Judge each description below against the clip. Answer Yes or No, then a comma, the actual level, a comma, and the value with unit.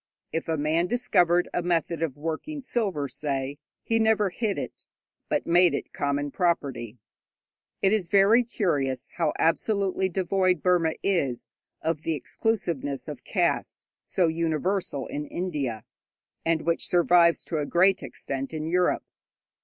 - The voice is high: No, medium, 170 Hz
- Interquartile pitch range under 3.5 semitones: No, average, 4.3 semitones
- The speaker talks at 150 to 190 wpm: No, average, 140 wpm